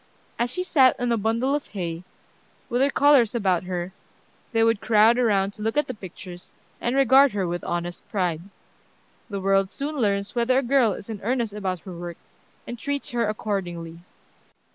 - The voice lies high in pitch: Yes, high, 215 Hz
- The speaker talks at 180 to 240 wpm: Yes, average, 185 wpm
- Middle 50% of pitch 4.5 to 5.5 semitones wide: Yes, average, 4.8 semitones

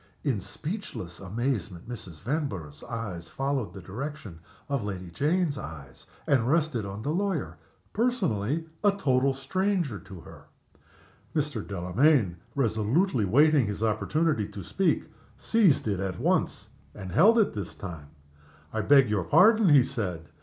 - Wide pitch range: Yes, wide, 8.0 semitones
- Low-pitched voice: Yes, low, 120 Hz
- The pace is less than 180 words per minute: Yes, average, 140 wpm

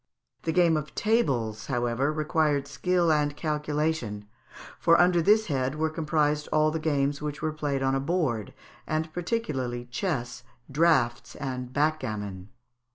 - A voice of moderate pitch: Yes, medium, 150 Hz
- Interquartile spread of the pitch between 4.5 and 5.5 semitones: No, average, 3.6 semitones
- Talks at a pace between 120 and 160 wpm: Yes, average, 140 wpm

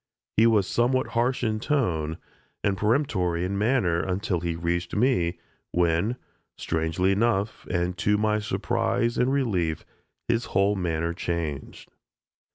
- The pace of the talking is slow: Yes, slow, 130 wpm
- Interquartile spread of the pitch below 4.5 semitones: No, average, 5.2 semitones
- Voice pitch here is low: Yes, very low, 95 Hz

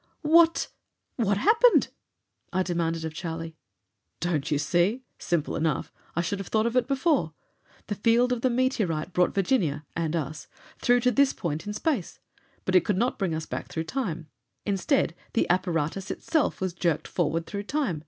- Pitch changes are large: Yes, wide, 7.0 semitones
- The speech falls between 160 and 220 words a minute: Yes, average, 175 wpm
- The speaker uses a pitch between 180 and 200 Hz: Yes, medium, 185 Hz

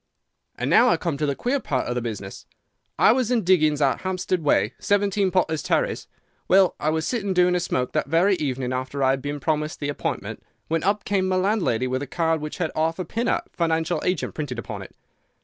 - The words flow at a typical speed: No, fast, 210 wpm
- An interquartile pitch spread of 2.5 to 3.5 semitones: No, average, 4.8 semitones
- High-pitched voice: No, medium, 165 Hz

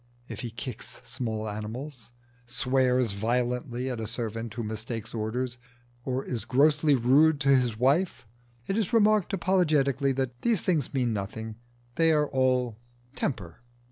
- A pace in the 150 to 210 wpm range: No, average, 140 wpm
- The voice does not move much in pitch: No, average, 3.8 semitones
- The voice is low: Yes, low, 125 Hz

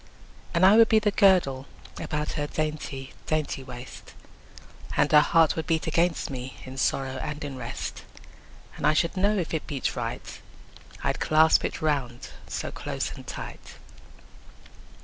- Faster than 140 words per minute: Yes, average, 160 wpm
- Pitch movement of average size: Yes, average, 3.8 semitones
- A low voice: No, medium, 155 Hz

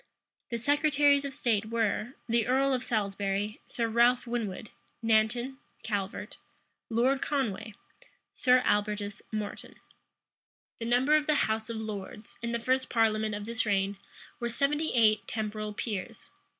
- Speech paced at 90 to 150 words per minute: Yes, slow, 135 wpm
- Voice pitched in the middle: No, high, 225 Hz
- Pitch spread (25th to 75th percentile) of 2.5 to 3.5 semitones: Yes, average, 3.0 semitones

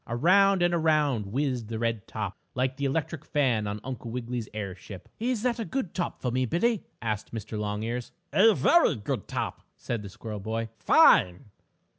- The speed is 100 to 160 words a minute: No, average, 175 wpm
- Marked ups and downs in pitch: Yes, wide, 7.0 semitones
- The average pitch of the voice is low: Yes, low, 125 Hz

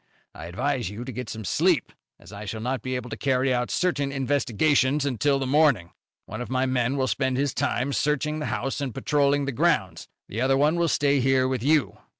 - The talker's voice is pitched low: Yes, low, 130 Hz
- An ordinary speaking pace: No, fast, 215 wpm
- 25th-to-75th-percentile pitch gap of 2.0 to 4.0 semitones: Yes, narrow, 2.6 semitones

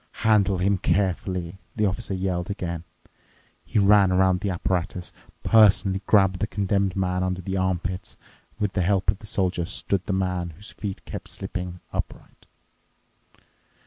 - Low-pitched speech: Yes, very low, 95 Hz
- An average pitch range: No, narrow, 1.6 semitones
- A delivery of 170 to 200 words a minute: No, average, 150 wpm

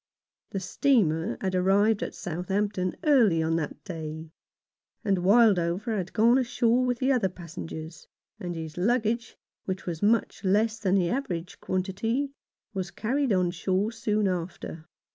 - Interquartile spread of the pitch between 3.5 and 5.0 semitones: Yes, average, 4.4 semitones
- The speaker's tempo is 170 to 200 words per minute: No, average, 145 wpm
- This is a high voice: Yes, high, 195 Hz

